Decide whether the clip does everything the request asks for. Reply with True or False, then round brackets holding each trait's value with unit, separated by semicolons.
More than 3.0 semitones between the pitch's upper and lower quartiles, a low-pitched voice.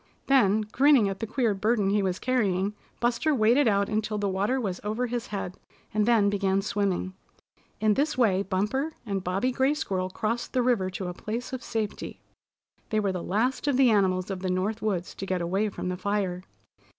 False (3.9 semitones; 210 Hz)